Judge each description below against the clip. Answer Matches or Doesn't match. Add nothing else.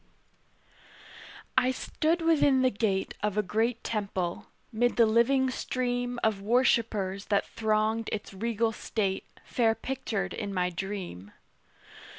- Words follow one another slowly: Matches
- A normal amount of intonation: Matches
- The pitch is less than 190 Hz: Doesn't match